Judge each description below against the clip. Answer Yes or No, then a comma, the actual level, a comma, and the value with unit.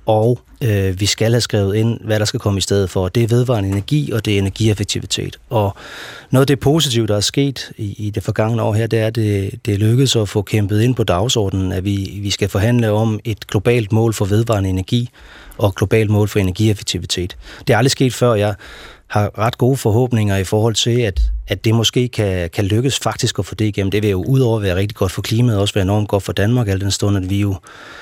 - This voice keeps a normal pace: No, fast, 245 wpm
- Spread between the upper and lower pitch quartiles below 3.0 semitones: Yes, narrow, 2.6 semitones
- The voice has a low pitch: Yes, low, 110 Hz